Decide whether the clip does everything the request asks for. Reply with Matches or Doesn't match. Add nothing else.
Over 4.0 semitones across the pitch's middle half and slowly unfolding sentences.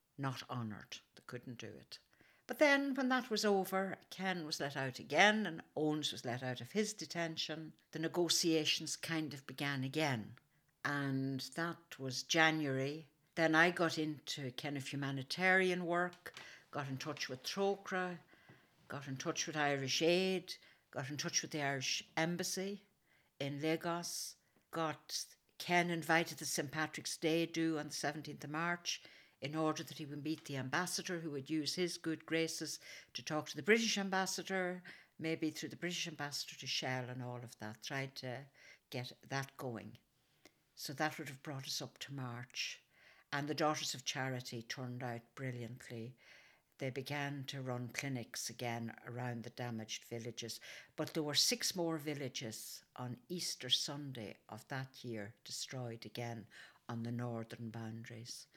Doesn't match